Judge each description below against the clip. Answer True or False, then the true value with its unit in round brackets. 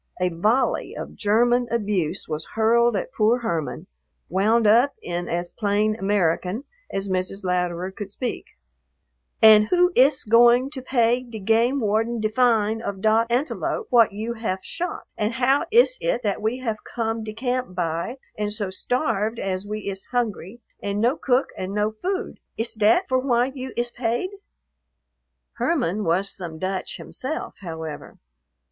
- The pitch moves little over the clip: False (3.9 semitones)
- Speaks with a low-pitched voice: False (220 Hz)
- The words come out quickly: False (160 wpm)